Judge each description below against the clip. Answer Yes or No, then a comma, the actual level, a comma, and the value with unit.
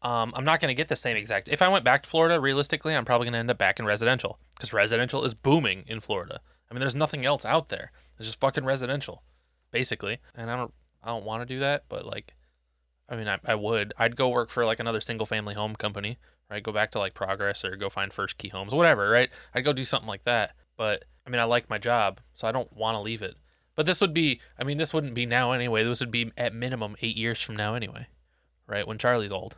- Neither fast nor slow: No, fast, 260 wpm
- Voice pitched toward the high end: No, low, 115 Hz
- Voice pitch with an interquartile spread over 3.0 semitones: Yes, average, 3.9 semitones